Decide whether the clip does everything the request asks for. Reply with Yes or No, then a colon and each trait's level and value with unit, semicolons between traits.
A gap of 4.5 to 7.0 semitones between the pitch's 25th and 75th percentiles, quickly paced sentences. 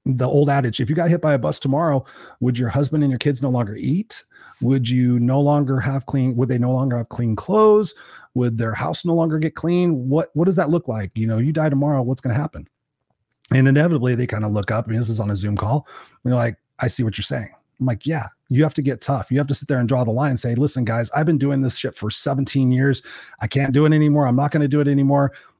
No: average, 3.0 semitones; fast, 280 wpm